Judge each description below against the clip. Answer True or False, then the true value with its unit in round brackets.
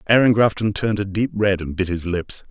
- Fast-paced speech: True (240 wpm)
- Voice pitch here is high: False (100 Hz)